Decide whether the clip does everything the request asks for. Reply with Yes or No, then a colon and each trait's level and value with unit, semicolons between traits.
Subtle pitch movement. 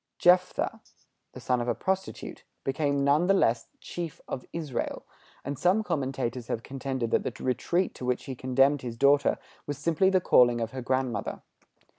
No: average, 5.0 semitones